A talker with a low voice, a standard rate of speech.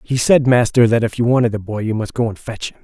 No: low, 115 Hz; fast, 320 wpm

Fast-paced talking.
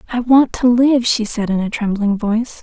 Yes: fast, 230 wpm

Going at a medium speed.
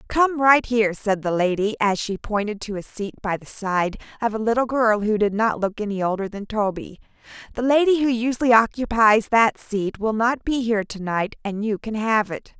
No: fast, 215 wpm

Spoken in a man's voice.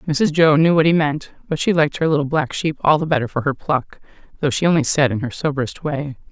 No: female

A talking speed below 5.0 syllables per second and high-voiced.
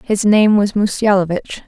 Yes: 4.4 syllables/s; high, 205 Hz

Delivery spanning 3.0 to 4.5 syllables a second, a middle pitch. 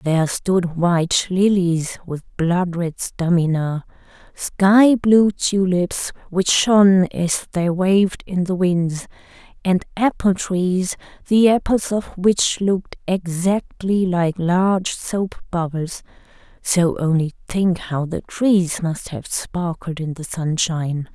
Yes: 3.5 syllables/s; medium, 180 Hz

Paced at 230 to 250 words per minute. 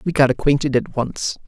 No: fast, 205 wpm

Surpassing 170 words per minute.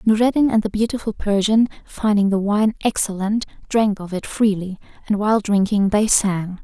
No: average, 165 wpm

